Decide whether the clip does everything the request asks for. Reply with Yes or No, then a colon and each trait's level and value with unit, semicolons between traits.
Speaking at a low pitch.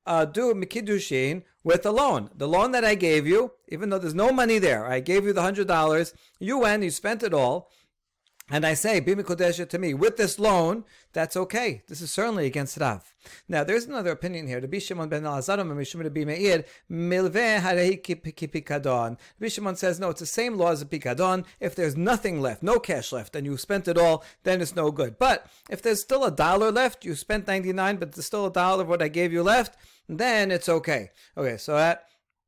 No: medium, 180 Hz